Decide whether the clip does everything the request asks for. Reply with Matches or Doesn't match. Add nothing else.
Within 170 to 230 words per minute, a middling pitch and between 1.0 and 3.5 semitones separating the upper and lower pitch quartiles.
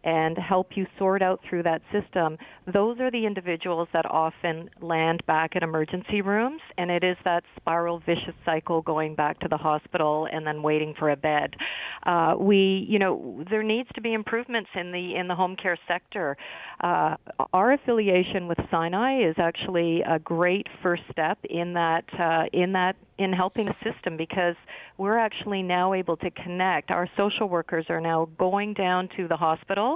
Matches